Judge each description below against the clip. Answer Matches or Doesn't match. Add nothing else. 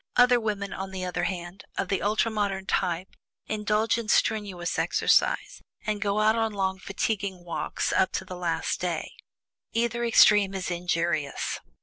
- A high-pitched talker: Matches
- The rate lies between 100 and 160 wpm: Matches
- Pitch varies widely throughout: Doesn't match